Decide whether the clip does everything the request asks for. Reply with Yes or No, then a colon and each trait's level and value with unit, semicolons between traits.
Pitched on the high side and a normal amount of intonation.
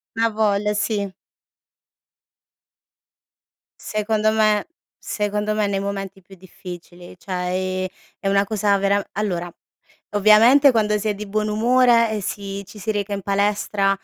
No: high, 205 Hz; narrow, 1.4 semitones